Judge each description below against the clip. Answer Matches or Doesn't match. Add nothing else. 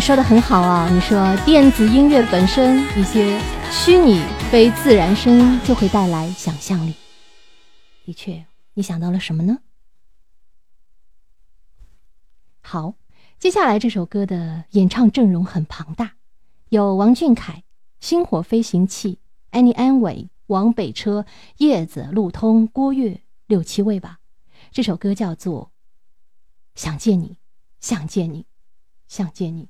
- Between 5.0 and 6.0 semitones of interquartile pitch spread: Matches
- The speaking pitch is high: Matches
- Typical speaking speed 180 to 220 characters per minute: Matches